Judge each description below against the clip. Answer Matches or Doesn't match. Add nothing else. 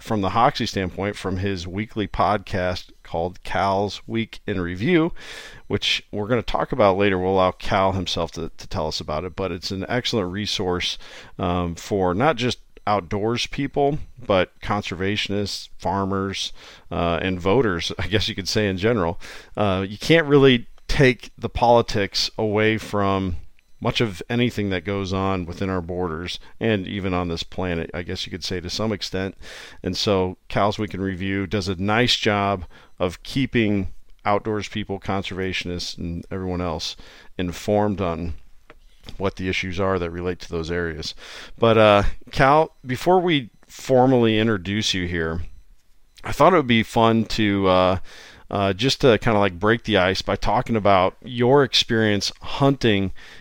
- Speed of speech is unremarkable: Matches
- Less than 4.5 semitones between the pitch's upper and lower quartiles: Matches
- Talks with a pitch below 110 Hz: Matches